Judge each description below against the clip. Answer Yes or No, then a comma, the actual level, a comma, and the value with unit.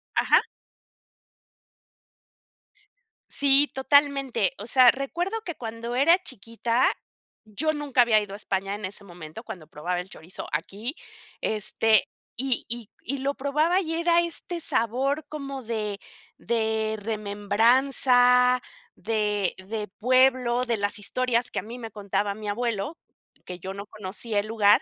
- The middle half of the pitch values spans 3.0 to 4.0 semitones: No, average, 4.6 semitones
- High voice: Yes, high, 230 Hz